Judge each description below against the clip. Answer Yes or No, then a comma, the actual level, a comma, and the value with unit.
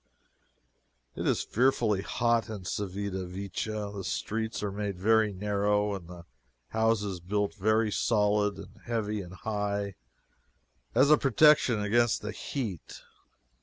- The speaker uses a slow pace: Yes, slow, 130 wpm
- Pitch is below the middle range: Yes, low, 105 Hz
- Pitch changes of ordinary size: No, narrow, 1.9 semitones